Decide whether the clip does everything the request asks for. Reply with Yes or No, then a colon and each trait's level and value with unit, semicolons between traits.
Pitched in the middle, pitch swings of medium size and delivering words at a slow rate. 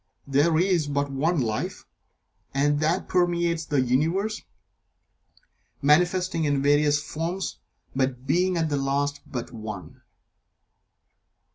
Yes: medium, 150 Hz; average, 3.9 semitones; slow, 110 wpm